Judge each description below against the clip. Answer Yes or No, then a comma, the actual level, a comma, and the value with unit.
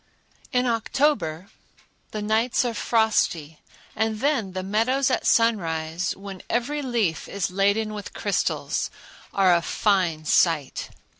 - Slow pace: Yes, slow, 125 wpm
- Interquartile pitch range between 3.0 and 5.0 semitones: Yes, average, 4.5 semitones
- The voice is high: Yes, high, 210 Hz